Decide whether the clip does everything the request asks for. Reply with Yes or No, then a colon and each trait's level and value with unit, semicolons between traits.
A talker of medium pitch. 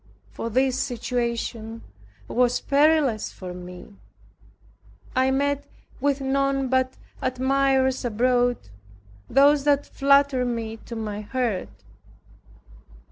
No: very high, 255 Hz